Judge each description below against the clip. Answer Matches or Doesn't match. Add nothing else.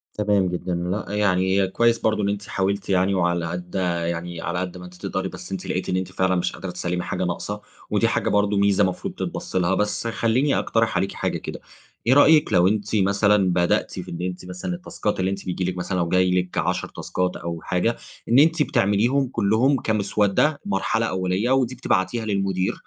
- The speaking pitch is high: Doesn't match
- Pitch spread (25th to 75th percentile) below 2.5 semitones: Doesn't match